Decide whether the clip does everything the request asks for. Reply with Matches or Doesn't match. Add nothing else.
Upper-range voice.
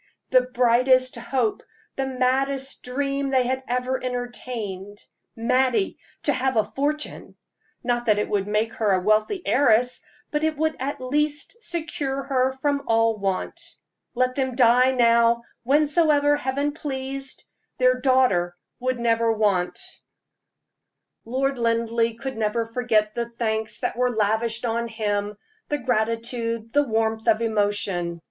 Matches